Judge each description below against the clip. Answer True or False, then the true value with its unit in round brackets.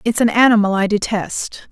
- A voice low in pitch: False (215 Hz)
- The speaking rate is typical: True (175 wpm)